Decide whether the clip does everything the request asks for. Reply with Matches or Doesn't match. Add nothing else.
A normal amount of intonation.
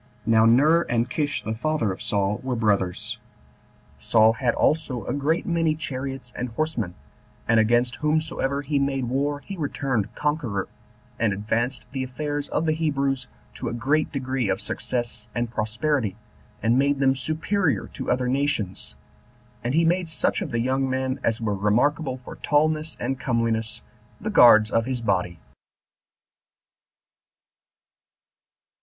Matches